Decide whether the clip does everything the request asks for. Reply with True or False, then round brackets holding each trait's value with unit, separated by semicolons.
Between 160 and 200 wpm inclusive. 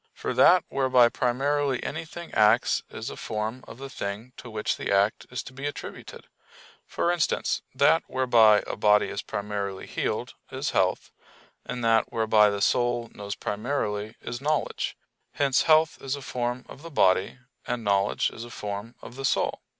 True (170 wpm)